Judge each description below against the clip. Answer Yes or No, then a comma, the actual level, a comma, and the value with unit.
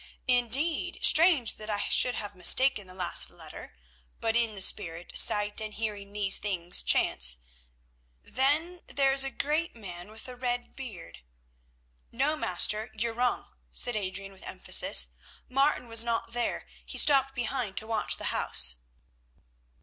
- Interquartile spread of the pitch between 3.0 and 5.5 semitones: Yes, average, 4.8 semitones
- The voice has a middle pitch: No, high, 225 Hz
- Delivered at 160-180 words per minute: No, average, 150 wpm